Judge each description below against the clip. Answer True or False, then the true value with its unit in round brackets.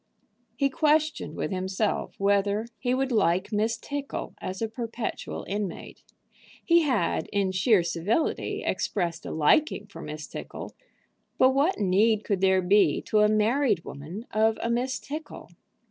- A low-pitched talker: False (215 Hz)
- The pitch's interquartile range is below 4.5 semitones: False (5.2 semitones)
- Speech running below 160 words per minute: True (145 wpm)